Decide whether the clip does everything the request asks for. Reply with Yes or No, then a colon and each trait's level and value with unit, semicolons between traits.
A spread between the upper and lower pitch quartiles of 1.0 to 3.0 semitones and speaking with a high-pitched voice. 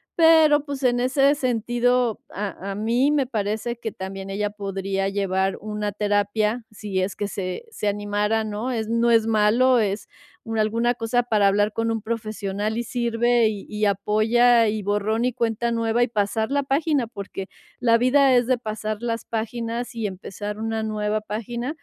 Yes: narrow, 2.6 semitones; high, 220 Hz